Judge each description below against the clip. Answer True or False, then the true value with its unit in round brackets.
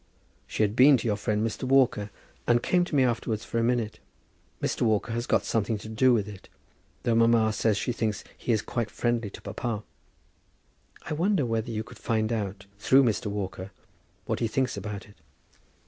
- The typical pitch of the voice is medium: False (115 Hz)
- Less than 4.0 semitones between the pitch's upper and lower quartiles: True (2.4 semitones)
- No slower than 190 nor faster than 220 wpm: True (195 wpm)